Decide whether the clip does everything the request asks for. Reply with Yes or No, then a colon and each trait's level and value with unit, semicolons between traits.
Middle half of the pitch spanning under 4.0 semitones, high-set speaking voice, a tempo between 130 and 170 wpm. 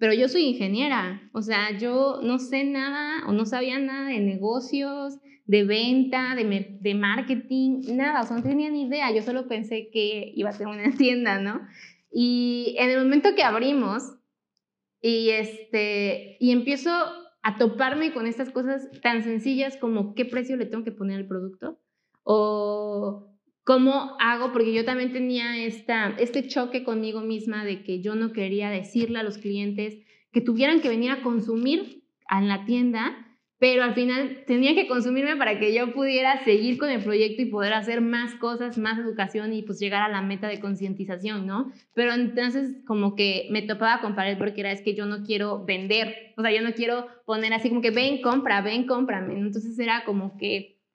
No: average, 3.5 semitones; high, 235 Hz; average, 185 wpm